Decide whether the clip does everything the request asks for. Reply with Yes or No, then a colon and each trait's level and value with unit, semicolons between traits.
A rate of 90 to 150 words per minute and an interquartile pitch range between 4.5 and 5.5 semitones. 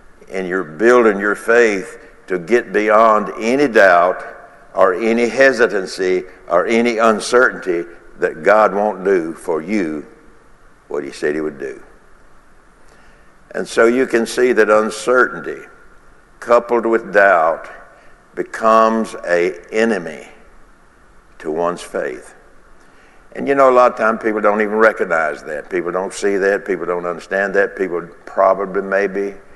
No: slow, 135 wpm; average, 3.1 semitones